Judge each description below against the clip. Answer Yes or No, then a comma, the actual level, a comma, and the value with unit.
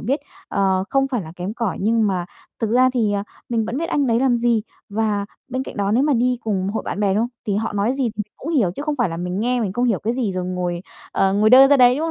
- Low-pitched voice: No, high, 225 Hz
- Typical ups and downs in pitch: Yes, average, 4.1 semitones